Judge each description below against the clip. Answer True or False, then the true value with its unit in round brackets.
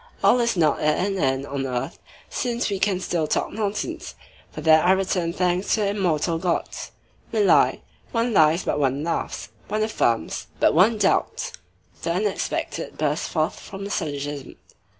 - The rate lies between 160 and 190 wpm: True (170 wpm)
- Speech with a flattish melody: False (5.3 semitones)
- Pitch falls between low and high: True (180 Hz)